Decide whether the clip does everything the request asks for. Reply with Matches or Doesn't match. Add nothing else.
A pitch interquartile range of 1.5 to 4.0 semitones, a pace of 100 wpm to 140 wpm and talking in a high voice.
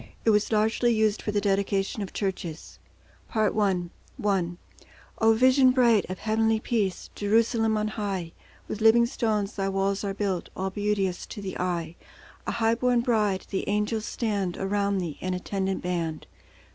Doesn't match